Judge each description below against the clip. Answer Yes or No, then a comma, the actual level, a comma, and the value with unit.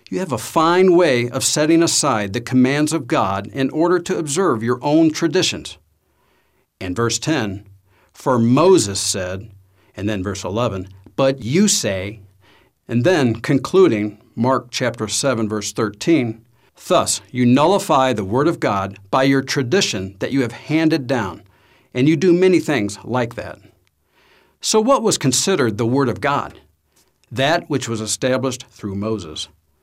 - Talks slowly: No, average, 155 wpm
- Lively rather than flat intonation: Yes, wide, 6.3 semitones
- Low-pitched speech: Yes, low, 120 Hz